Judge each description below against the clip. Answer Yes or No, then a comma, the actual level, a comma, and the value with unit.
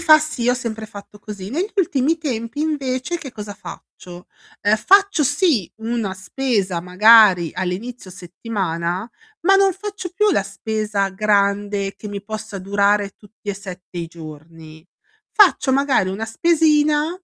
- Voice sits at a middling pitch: No, high, 215 Hz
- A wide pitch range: Yes, wide, 6.8 semitones